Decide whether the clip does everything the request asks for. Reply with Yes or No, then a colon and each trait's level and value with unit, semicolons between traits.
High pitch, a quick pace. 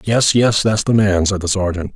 No: low, 100 Hz; fast, 245 wpm